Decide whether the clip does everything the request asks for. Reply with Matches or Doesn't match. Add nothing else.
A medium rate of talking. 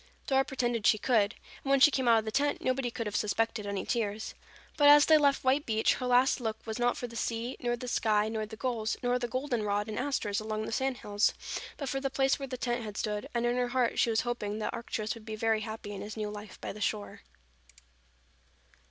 Doesn't match